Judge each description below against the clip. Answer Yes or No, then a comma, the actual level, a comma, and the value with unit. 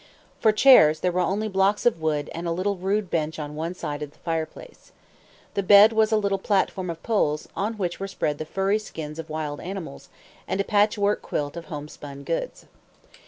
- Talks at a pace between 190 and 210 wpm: Yes, average, 195 wpm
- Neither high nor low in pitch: Yes, medium, 180 Hz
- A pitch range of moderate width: Yes, average, 4.6 semitones